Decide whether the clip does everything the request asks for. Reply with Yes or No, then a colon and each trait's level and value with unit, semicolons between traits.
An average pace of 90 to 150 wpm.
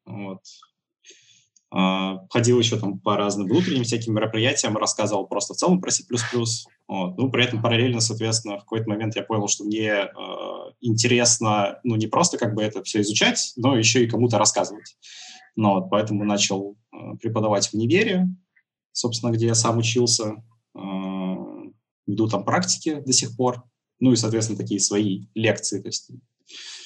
No: fast, 160 wpm